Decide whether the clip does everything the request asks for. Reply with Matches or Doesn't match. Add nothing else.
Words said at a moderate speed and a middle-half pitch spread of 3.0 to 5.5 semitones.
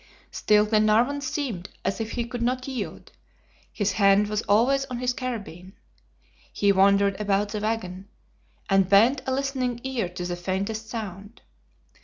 Matches